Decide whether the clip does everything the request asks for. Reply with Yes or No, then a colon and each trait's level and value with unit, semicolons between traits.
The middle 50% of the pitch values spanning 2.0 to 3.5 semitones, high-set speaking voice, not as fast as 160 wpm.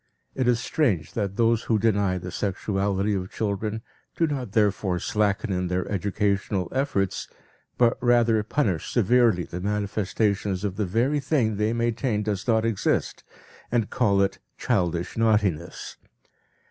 No: average, 3.1 semitones; low, 105 Hz; average, 140 wpm